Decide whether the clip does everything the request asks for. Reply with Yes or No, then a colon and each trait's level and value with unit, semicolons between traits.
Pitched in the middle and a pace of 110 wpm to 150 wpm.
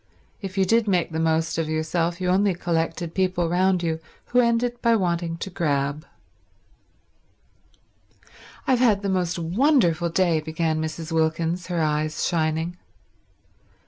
Yes: medium, 170 Hz; average, 140 wpm